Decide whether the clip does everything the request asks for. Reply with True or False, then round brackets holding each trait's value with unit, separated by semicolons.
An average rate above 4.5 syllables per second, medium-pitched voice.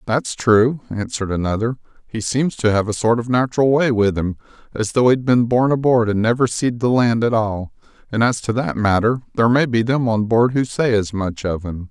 False (5.3 syllables/s; 115 Hz)